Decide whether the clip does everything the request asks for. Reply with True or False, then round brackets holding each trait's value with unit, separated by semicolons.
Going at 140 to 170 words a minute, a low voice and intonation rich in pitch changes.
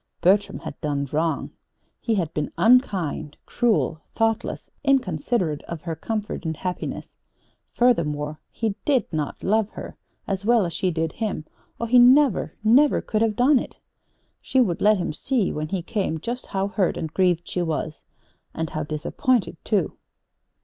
False (160 wpm; 190 Hz; 6.1 semitones)